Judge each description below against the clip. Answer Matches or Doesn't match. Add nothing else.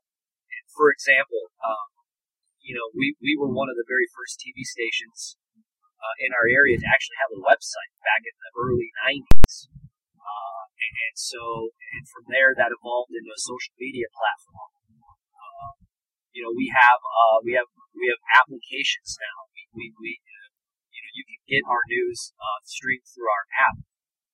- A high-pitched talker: Matches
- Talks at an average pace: Matches